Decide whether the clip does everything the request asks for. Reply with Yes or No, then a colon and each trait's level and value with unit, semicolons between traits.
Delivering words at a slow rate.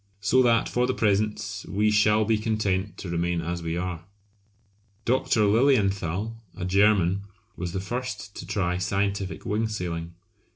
No: average, 150 wpm